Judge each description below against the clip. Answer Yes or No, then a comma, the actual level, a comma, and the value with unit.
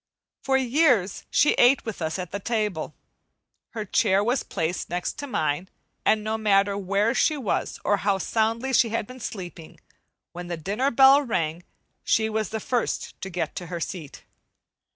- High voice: Yes, high, 210 Hz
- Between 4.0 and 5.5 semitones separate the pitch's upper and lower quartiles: Yes, average, 4.8 semitones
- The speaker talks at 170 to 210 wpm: Yes, average, 175 wpm